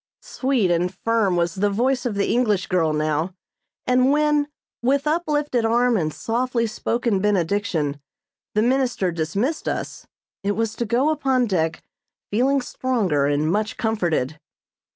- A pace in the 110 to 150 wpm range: Yes, average, 140 wpm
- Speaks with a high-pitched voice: Yes, high, 220 Hz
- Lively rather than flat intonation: Yes, wide, 6.1 semitones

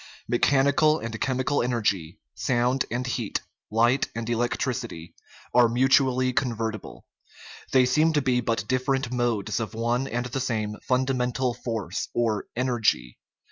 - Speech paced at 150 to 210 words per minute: No, slow, 135 wpm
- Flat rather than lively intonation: Yes, narrow, 2.3 semitones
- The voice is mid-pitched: No, low, 125 Hz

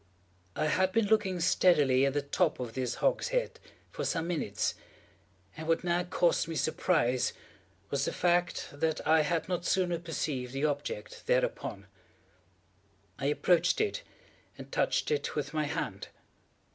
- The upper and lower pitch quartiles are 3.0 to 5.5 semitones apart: Yes, average, 3.9 semitones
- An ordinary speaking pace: Yes, average, 145 wpm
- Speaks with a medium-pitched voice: Yes, medium, 160 Hz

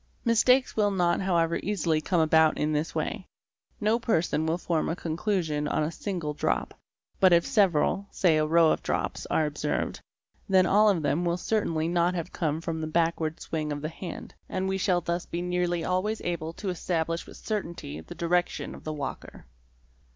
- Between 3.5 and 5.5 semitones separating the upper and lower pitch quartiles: No, average, 2.9 semitones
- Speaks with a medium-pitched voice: Yes, medium, 170 Hz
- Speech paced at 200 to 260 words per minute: No, average, 190 wpm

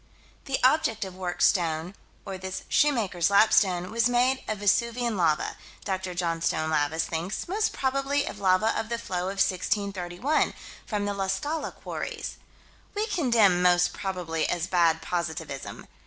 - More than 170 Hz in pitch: Yes, high, 190 Hz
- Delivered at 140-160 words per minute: Yes, average, 145 wpm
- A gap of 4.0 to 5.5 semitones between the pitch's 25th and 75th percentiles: Yes, average, 5.0 semitones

